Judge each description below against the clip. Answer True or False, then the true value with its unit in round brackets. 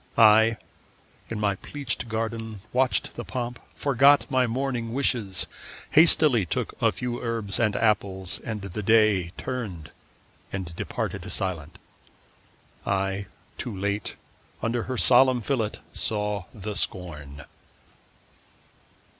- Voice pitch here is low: True (110 Hz)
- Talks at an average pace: False (115 wpm)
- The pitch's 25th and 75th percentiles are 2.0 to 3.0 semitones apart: False (3.8 semitones)